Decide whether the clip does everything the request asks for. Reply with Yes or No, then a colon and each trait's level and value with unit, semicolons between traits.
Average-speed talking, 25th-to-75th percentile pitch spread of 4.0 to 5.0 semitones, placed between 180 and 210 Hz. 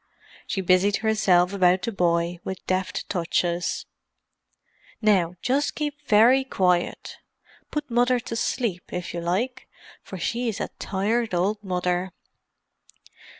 No: slow, 115 wpm; average, 4.4 semitones; high, 190 Hz